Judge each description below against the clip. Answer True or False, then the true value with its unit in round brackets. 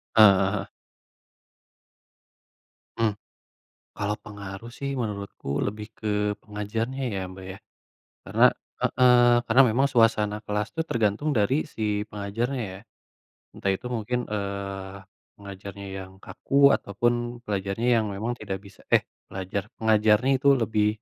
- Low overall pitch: True (105 Hz)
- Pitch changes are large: False (3.2 semitones)